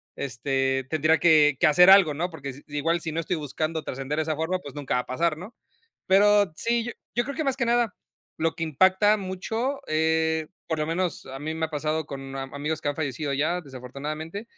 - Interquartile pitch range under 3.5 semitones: No, average, 4.1 semitones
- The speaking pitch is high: No, medium, 160 Hz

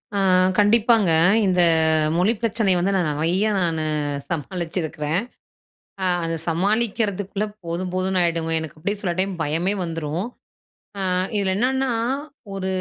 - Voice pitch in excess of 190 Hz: No, medium, 185 Hz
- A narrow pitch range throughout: No, average, 3.5 semitones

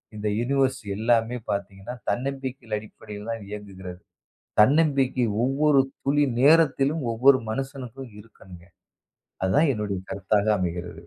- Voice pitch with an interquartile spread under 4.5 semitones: No, average, 4.8 semitones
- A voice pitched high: No, low, 120 Hz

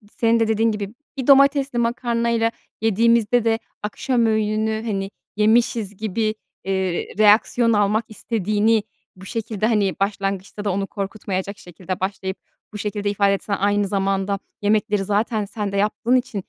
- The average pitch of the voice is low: No, high, 210 Hz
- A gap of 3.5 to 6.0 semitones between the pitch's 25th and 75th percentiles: No, narrow, 2.4 semitones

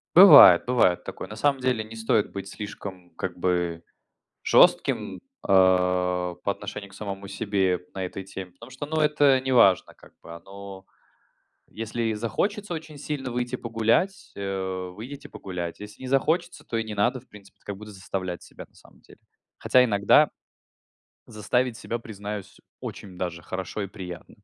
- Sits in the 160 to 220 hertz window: No, low, 105 Hz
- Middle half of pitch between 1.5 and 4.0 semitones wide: No, average, 4.8 semitones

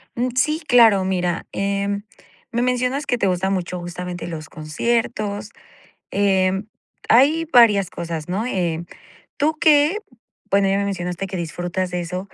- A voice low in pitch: No, high, 195 Hz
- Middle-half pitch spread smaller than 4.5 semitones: No, average, 4.9 semitones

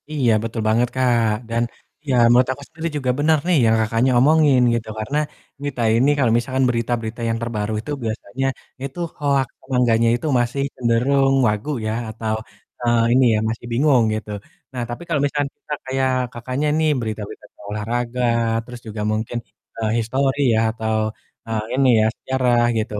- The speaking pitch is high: No, low, 120 Hz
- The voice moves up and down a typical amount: Yes, average, 3.0 semitones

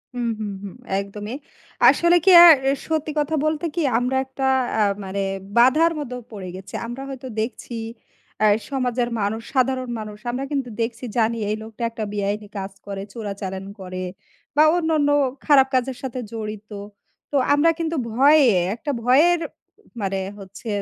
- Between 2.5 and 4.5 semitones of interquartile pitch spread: No, average, 5.0 semitones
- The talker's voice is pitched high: Yes, high, 245 Hz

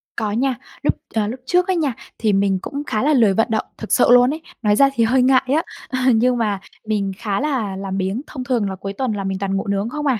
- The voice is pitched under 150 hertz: No, high, 225 Hz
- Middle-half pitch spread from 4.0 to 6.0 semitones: Yes, average, 4.6 semitones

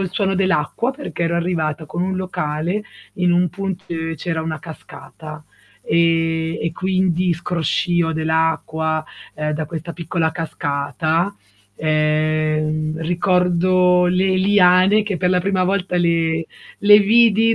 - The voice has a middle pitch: Yes, medium, 170 Hz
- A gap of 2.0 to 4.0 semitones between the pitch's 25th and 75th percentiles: Yes, narrow, 2.6 semitones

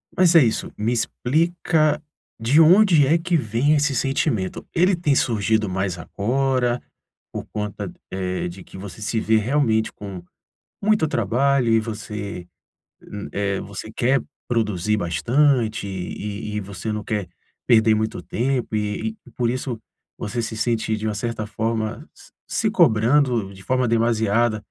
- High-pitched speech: No, low, 110 Hz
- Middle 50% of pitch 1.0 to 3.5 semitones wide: No, average, 4.0 semitones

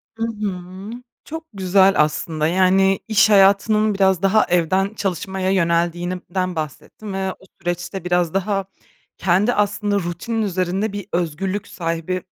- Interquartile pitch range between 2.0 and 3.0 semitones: Yes, narrow, 2.4 semitones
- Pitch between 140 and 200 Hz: Yes, high, 190 Hz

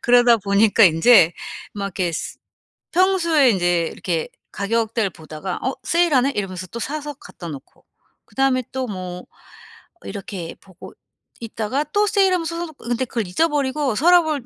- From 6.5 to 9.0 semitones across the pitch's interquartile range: Yes, wide, 7.8 semitones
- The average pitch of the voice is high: Yes, high, 230 Hz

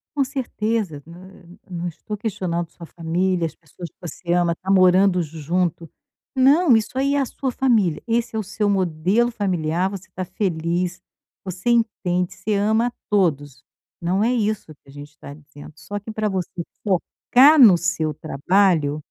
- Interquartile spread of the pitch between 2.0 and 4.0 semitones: No, average, 4.5 semitones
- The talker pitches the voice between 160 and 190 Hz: Yes, medium, 185 Hz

